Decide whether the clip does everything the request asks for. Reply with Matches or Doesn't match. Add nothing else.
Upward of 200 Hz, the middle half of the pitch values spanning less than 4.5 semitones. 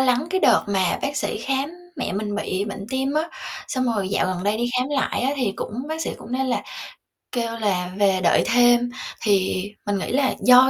Doesn't match